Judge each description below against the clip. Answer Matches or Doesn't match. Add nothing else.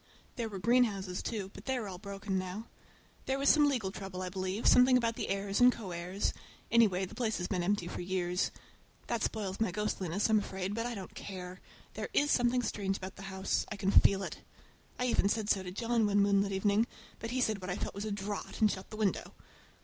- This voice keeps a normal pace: Doesn't match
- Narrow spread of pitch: Doesn't match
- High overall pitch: Matches